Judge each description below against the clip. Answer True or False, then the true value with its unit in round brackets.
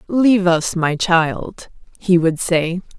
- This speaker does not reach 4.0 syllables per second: True (3.3 syllables/s)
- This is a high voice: False (175 Hz)